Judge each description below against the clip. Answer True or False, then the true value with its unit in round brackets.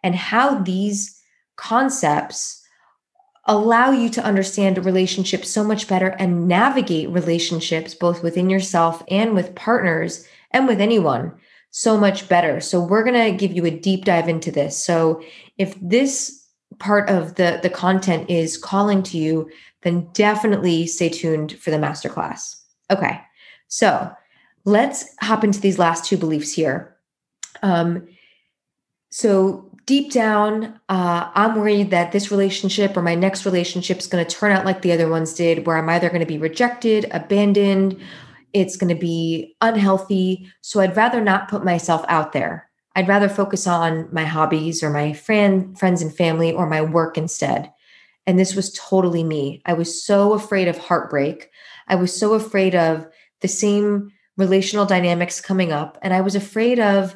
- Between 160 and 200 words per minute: True (165 wpm)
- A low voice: False (185 Hz)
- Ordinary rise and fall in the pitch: True (3.2 semitones)